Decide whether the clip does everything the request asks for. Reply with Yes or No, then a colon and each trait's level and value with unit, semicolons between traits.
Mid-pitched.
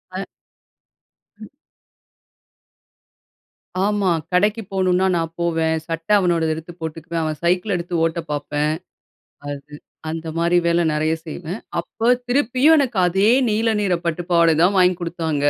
Yes: medium, 170 Hz